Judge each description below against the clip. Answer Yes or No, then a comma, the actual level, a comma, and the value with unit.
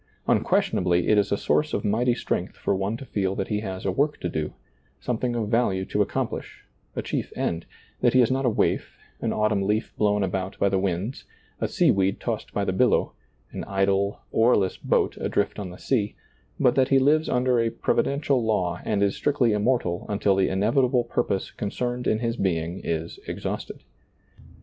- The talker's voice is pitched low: Yes, low, 105 Hz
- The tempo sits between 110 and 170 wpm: No, average, 195 wpm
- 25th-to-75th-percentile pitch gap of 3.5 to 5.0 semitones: Yes, average, 4.1 semitones